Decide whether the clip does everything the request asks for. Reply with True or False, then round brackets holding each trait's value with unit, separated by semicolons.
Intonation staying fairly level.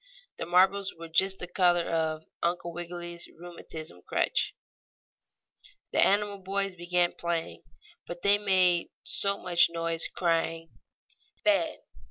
True (2.3 semitones)